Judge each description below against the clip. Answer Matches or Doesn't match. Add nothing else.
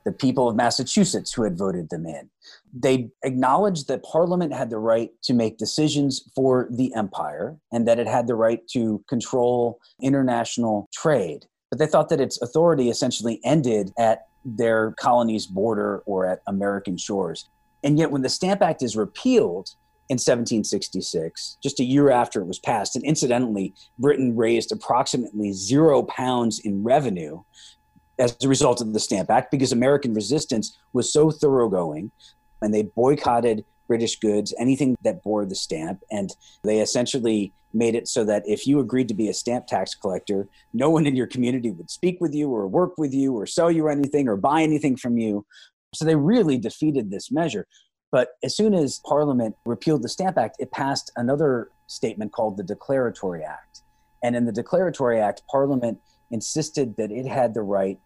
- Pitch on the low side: Matches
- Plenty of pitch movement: Doesn't match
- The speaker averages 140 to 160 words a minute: Doesn't match